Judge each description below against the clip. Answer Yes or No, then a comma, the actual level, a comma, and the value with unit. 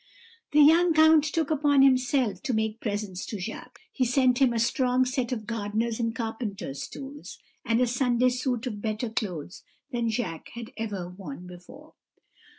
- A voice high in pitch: Yes, high, 235 Hz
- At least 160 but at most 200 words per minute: Yes, average, 165 wpm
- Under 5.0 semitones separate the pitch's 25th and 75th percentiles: Yes, average, 3.5 semitones